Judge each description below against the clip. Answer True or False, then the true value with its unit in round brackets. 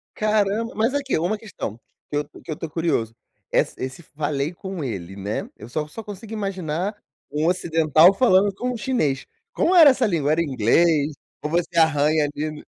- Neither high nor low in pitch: True (165 Hz)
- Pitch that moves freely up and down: True (5.7 semitones)